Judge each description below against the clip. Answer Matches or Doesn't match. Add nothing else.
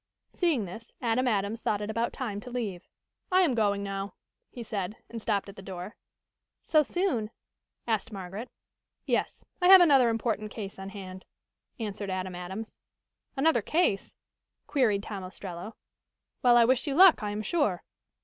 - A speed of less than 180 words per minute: Matches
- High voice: Matches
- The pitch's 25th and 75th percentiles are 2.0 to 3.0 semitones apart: Doesn't match